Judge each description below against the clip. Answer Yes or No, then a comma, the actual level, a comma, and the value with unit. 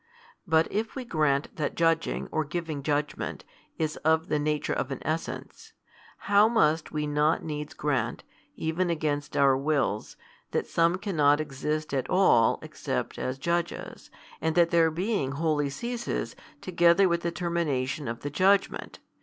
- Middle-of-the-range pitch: Yes, medium, 155 Hz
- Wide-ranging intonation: No, average, 2.8 semitones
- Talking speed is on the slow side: No, average, 150 wpm